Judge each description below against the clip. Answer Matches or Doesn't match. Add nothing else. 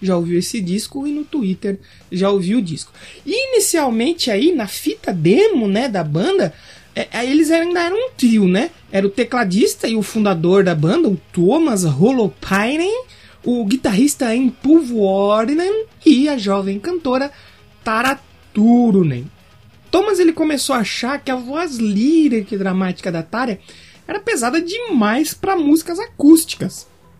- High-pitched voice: Matches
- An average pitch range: Doesn't match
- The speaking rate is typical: Matches